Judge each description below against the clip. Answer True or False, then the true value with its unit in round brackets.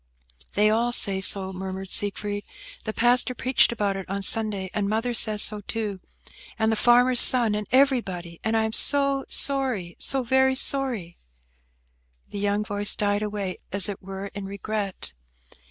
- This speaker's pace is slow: False (160 wpm)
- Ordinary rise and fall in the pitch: True (3.4 semitones)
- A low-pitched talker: False (210 Hz)